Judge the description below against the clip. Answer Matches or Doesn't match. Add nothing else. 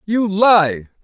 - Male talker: Matches